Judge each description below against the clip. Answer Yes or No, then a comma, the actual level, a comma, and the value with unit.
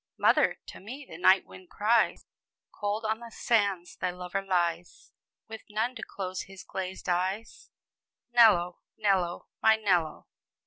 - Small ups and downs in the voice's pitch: No, average, 3.4 semitones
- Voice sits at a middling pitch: No, high, 195 Hz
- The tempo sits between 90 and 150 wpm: Yes, average, 140 wpm